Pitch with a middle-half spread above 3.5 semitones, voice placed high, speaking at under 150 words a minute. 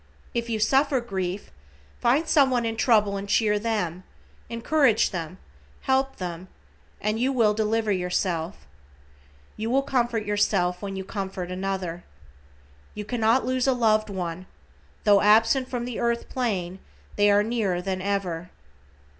Yes: average, 4.0 semitones; high, 210 Hz; average, 140 wpm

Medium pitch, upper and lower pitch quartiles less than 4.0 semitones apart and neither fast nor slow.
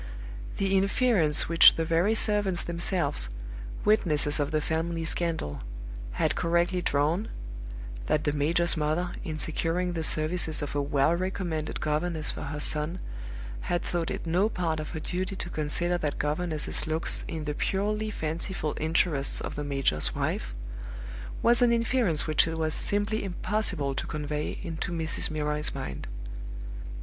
Yes: medium, 165 Hz; average, 3.1 semitones; average, 150 wpm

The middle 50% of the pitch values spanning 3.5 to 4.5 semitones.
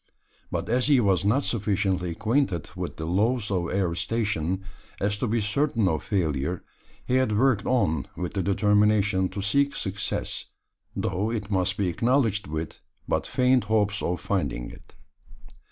Yes: average, 3.8 semitones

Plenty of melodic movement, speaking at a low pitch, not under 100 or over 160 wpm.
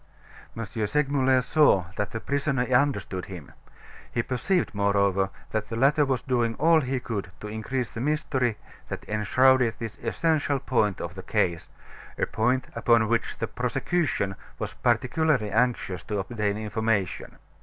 No: average, 4.3 semitones; low, 115 Hz; average, 145 wpm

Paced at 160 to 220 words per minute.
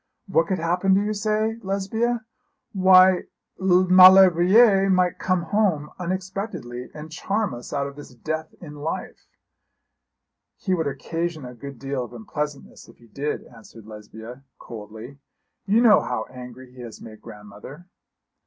No: average, 145 wpm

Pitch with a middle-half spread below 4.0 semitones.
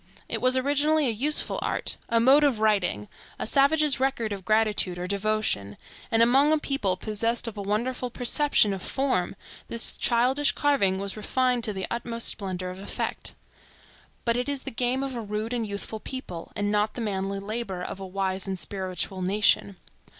No: average, 4.6 semitones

